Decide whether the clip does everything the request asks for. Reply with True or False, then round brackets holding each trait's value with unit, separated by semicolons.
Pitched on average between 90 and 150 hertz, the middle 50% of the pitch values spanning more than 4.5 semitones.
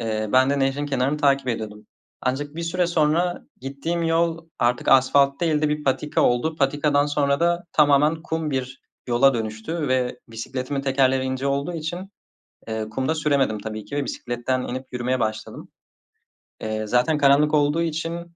False (140 Hz; 3.4 semitones)